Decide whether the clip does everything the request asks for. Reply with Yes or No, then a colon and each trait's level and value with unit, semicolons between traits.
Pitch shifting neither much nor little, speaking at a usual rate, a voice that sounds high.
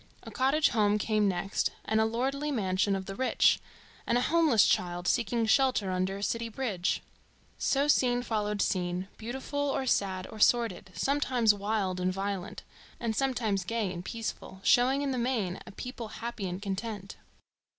Yes: average, 4.4 semitones; average, 165 wpm; high, 220 Hz